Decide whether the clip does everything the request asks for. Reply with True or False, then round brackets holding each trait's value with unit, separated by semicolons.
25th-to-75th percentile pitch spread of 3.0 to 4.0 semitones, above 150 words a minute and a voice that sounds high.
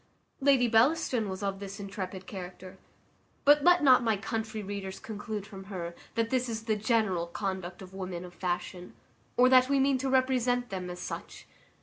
False (4.8 semitones; 180 wpm; 210 Hz)